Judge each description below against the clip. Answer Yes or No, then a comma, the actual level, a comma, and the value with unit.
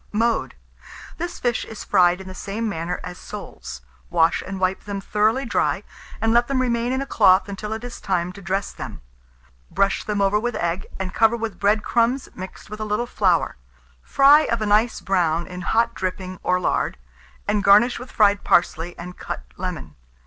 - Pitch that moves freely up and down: No, average, 3.8 semitones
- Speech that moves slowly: No, average, 190 wpm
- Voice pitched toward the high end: Yes, high, 205 Hz